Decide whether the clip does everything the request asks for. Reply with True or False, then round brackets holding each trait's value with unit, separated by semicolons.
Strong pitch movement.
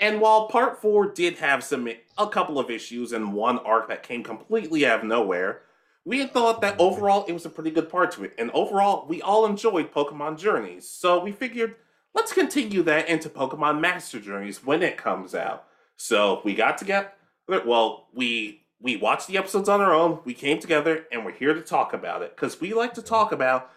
True (8.3 semitones)